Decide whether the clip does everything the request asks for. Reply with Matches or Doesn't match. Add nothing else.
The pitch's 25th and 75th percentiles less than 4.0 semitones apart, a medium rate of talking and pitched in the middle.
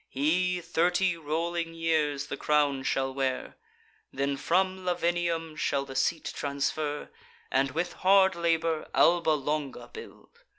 Doesn't match